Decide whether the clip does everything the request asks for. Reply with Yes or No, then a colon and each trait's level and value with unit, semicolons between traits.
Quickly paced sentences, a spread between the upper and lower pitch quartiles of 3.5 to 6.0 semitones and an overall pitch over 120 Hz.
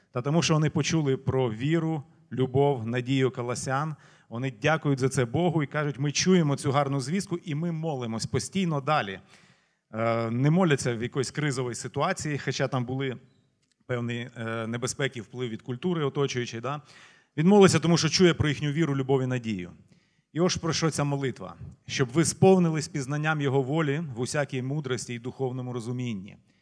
Yes: fast, 160 wpm; average, 3.8 semitones; medium, 140 Hz